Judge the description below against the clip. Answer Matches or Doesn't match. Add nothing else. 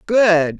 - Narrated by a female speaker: Matches